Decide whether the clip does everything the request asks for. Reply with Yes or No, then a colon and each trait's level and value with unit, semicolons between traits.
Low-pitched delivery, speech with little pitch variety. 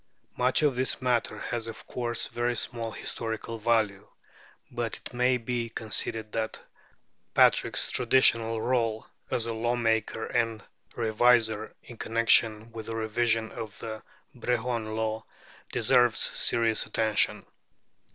Yes: low, 115 Hz; narrow, 1.5 semitones